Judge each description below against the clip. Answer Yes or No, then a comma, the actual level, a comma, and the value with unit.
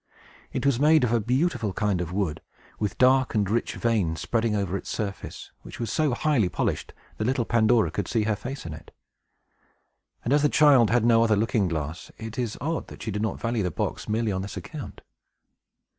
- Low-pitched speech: Yes, low, 110 Hz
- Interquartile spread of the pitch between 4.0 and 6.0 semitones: No, average, 3.5 semitones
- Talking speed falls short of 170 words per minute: No, fast, 205 wpm